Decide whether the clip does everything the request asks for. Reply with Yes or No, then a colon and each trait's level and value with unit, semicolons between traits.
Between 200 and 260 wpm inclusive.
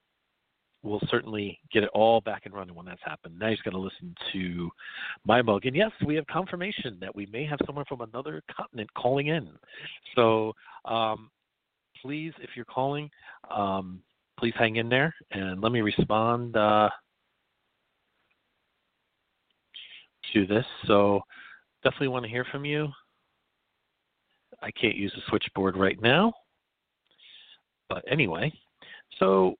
No: average, 140 wpm